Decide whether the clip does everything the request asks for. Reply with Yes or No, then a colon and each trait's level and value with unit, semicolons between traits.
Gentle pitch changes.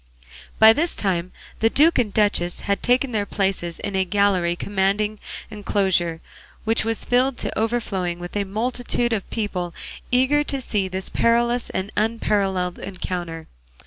No: average, 3.7 semitones